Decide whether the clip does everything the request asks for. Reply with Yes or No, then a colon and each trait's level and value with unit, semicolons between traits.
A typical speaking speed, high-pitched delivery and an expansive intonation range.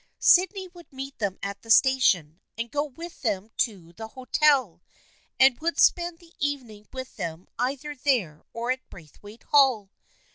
Yes: average, 155 wpm; very high, 255 Hz; wide, 5.9 semitones